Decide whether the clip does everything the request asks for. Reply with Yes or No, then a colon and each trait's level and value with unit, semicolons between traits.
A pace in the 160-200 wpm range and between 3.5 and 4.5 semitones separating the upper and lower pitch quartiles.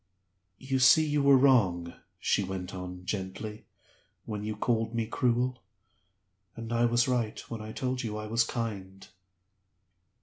No: average, 145 wpm; average, 3.8 semitones